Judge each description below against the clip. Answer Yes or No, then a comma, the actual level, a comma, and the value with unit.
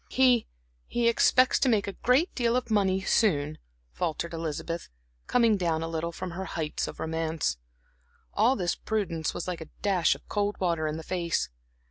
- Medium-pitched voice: Yes, medium, 180 Hz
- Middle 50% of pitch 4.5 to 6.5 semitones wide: Yes, average, 5.1 semitones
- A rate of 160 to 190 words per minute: Yes, average, 175 wpm